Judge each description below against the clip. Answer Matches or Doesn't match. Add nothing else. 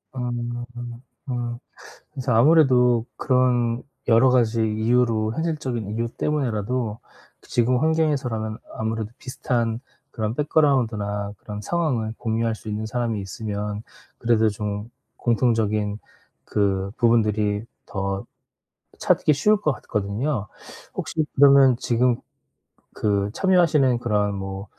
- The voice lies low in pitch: Matches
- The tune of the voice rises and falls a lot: Doesn't match